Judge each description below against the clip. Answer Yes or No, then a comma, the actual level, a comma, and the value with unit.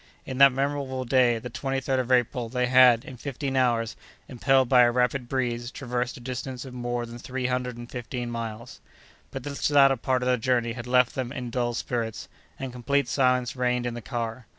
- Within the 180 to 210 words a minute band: Yes, average, 200 wpm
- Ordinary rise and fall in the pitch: No, narrow, 1.5 semitones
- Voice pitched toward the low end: Yes, low, 125 Hz